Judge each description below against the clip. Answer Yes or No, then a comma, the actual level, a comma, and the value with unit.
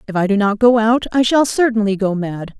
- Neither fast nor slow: No, fast, 255 wpm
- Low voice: No, high, 220 Hz